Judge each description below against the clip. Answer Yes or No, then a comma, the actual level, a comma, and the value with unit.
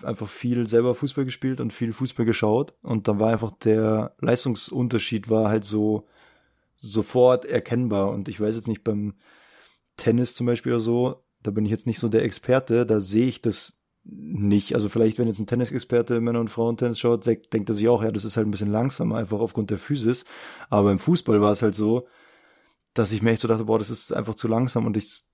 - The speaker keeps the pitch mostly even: Yes, narrow, 1.9 semitones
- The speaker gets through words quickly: Yes, fast, 215 wpm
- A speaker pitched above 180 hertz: No, low, 115 Hz